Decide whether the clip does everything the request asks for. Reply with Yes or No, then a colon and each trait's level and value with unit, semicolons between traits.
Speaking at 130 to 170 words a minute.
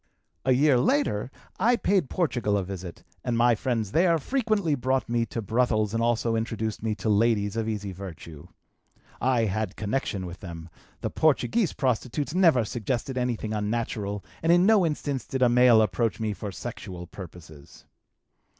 Yes: average, 160 wpm